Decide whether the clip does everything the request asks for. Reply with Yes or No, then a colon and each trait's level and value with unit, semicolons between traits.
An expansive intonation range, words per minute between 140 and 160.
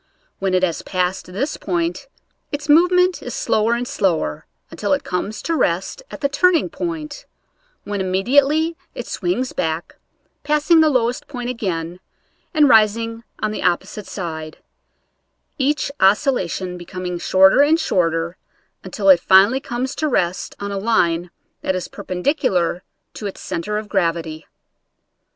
Yes: wide, 7.7 semitones; average, 145 wpm